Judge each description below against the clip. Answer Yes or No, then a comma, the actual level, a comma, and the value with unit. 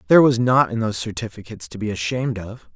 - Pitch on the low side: Yes, low, 115 Hz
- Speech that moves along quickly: Yes, fast, 220 wpm